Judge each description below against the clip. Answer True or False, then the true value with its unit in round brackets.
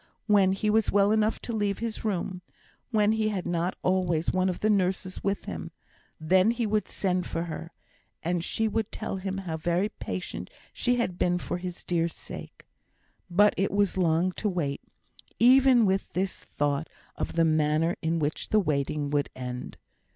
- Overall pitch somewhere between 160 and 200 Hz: True (185 Hz)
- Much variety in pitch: False (3.8 semitones)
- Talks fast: False (180 wpm)